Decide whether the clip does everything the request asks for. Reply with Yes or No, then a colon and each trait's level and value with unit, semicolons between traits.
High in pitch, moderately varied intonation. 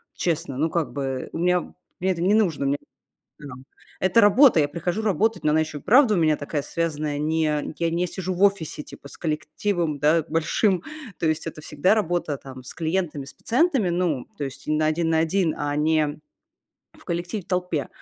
No: medium, 165 Hz; average, 3.3 semitones